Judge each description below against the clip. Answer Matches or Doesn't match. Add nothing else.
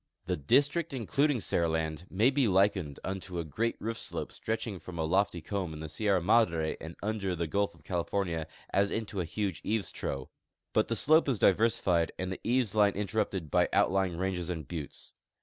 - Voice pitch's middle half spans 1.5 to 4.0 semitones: Doesn't match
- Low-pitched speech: Matches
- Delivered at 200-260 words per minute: Doesn't match